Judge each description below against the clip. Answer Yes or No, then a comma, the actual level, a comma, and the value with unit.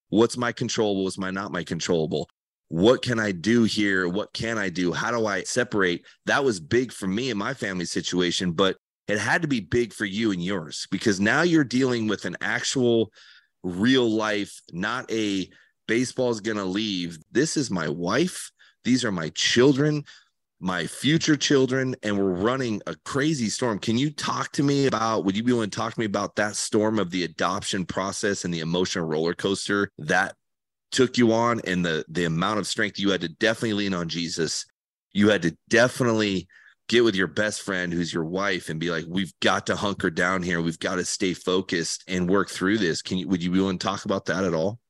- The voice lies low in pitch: Yes, low, 100 Hz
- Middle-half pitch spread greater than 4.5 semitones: No, average, 4.1 semitones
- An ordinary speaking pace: No, fast, 210 wpm